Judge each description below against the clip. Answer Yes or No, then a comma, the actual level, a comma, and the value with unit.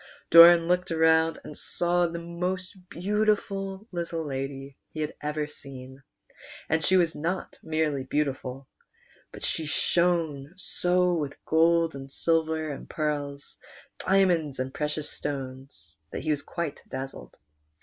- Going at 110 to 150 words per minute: Yes, average, 140 wpm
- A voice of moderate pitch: Yes, medium, 160 Hz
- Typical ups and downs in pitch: Yes, average, 3.4 semitones